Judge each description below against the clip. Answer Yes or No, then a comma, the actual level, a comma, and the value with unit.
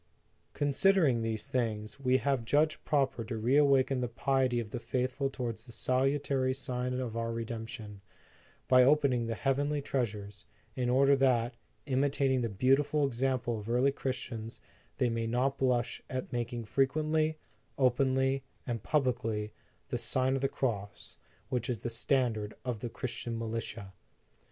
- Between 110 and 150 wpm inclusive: Yes, average, 145 wpm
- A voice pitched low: Yes, low, 125 Hz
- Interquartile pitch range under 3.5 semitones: Yes, average, 2.8 semitones